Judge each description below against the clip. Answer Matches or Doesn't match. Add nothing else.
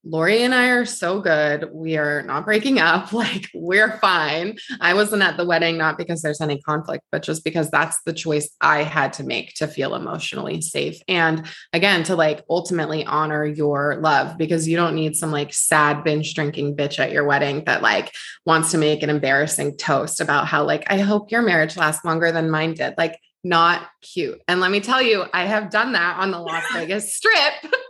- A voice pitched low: Doesn't match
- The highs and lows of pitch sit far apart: Doesn't match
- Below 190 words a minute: Doesn't match